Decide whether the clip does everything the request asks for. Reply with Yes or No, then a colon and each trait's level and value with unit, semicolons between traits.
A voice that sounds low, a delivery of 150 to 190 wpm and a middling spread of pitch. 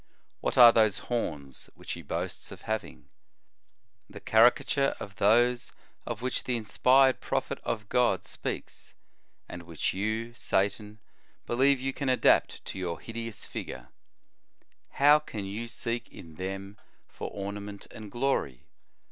No: low, 110 Hz; average, 140 wpm; average, 3.9 semitones